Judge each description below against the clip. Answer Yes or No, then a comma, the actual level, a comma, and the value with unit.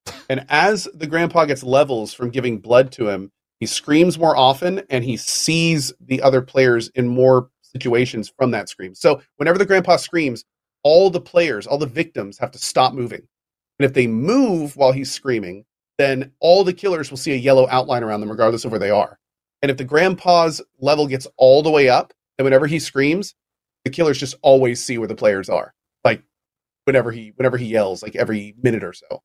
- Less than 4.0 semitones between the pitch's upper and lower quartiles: No, average, 4.6 semitones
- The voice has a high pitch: No, low, 130 Hz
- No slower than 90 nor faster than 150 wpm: No, fast, 205 wpm